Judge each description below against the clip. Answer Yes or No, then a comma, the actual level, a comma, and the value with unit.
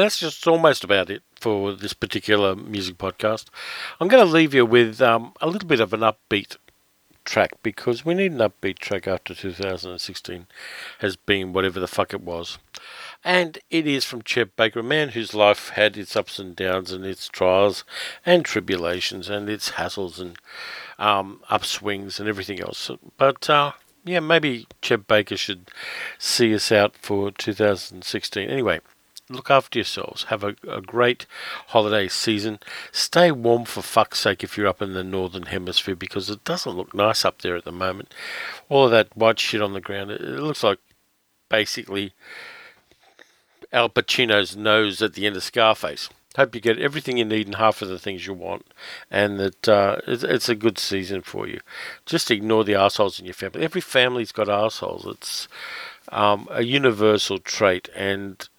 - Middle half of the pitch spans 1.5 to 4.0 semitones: Yes, average, 3.4 semitones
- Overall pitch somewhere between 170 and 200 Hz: No, low, 105 Hz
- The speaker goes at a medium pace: Yes, average, 175 wpm